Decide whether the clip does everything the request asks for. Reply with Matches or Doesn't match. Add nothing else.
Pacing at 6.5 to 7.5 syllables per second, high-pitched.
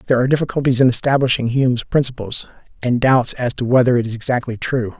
Doesn't match